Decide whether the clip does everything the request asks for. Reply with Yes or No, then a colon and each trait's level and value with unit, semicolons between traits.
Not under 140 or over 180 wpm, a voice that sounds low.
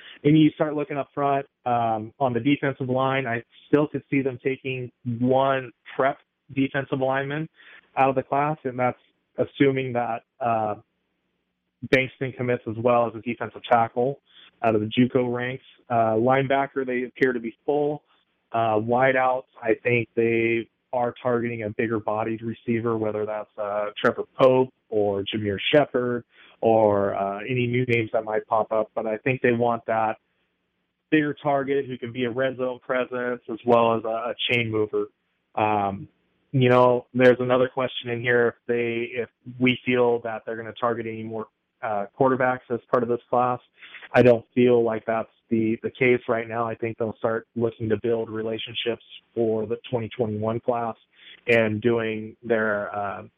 Yes: average, 175 wpm; low, 120 Hz